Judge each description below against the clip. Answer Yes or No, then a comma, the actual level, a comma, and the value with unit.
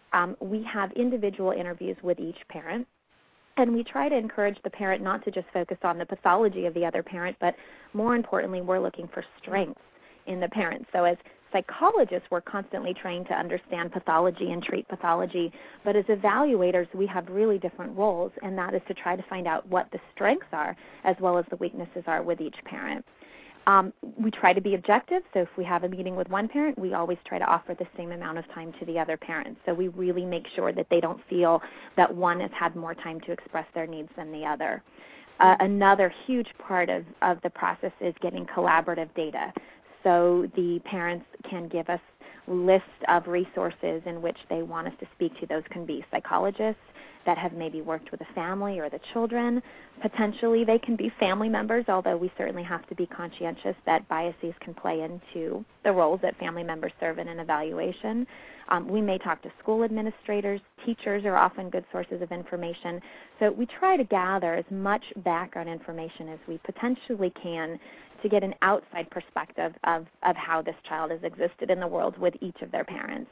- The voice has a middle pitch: Yes, medium, 180 Hz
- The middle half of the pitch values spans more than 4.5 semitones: No, average, 3.2 semitones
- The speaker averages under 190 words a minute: No, average, 200 wpm